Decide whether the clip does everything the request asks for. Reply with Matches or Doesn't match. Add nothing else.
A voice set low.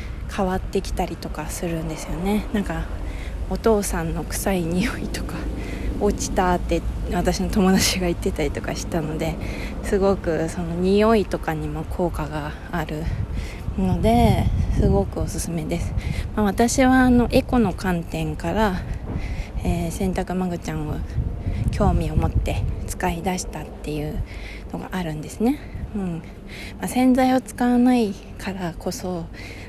Doesn't match